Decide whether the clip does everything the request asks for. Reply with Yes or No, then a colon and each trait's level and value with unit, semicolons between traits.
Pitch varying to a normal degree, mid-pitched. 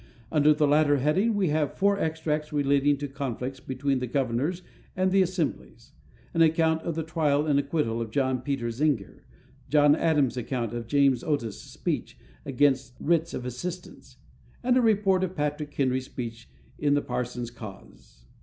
Yes: average, 4.1 semitones; medium, 145 Hz